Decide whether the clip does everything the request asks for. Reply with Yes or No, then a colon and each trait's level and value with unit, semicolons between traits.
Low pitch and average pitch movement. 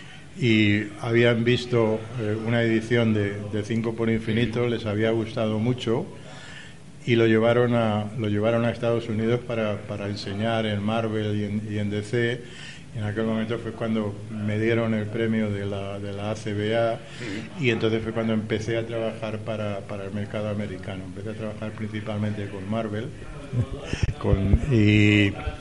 No: low, 110 Hz; narrow, 1.9 semitones